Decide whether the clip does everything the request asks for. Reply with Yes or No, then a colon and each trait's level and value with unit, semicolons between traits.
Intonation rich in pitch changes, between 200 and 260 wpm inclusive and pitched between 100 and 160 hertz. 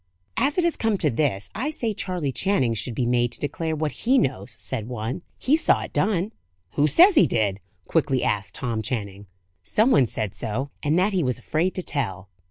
Yes: wide, 9.0 semitones; fast, 205 wpm; medium, 140 Hz